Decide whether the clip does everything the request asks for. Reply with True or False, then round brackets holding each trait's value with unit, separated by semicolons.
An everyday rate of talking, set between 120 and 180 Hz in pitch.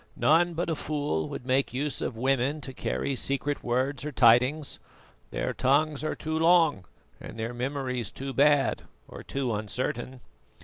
True (160 wpm; 135 Hz)